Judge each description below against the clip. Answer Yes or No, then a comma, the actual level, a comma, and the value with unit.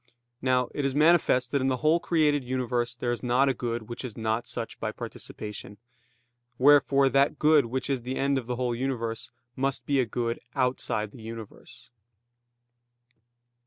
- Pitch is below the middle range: Yes, low, 125 Hz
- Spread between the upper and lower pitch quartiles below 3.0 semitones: Yes, narrow, 2.6 semitones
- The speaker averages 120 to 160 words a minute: No, average, 170 wpm